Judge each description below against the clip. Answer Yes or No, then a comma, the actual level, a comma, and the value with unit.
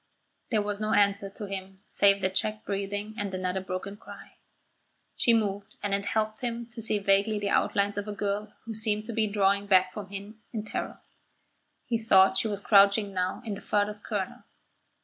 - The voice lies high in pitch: Yes, high, 205 Hz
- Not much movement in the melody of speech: Yes, narrow, 1.4 semitones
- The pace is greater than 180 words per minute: Yes, average, 190 wpm